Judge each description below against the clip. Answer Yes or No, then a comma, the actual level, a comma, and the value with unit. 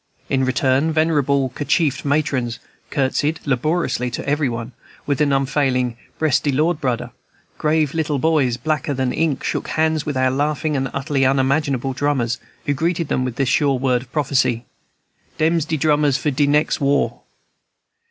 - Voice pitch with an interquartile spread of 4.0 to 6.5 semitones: No, average, 2.8 semitones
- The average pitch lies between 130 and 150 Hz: Yes, medium, 140 Hz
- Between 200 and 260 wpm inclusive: No, average, 160 wpm